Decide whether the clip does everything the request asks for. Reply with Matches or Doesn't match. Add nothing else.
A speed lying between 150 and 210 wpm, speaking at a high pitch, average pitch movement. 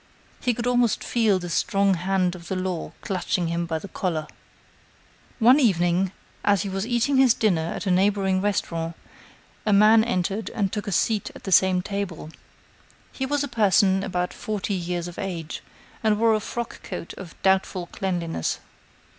Matches